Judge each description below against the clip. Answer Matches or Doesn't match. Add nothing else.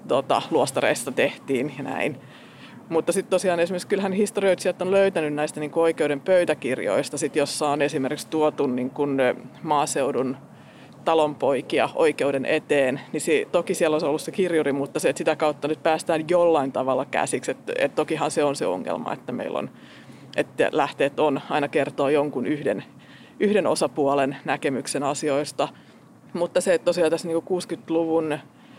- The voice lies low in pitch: Doesn't match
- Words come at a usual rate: Matches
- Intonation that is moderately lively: Matches